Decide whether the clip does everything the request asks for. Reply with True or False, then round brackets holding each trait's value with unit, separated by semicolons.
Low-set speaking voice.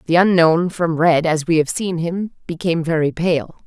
False (165 Hz)